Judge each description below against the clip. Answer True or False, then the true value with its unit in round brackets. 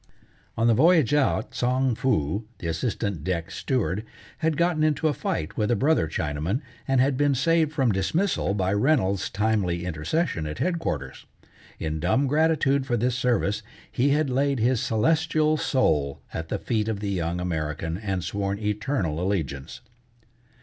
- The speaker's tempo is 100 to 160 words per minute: True (155 wpm)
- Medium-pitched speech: False (110 Hz)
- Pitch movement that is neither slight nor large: False (7.8 semitones)